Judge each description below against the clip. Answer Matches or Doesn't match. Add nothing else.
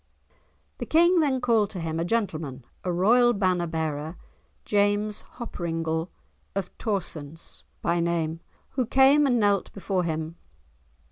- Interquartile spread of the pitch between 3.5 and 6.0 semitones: Matches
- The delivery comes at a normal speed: Doesn't match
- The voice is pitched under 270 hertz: Matches